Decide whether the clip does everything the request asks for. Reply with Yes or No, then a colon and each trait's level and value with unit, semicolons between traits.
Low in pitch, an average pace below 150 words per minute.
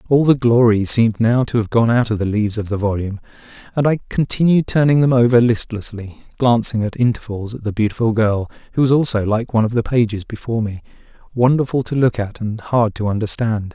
No: low, 115 Hz; fast, 205 wpm